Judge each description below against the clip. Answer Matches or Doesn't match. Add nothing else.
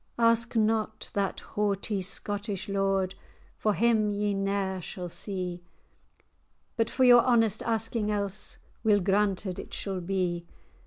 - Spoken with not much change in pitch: Matches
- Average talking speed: Doesn't match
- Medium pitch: Doesn't match